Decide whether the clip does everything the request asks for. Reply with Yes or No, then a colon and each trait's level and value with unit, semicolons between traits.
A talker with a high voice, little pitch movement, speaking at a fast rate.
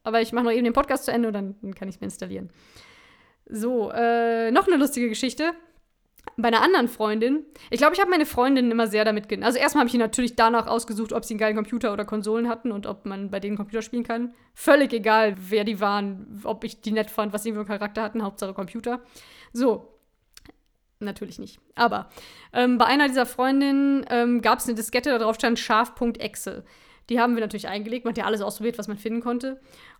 Yes: high, 230 Hz; narrow, 2.2 semitones; fast, 220 wpm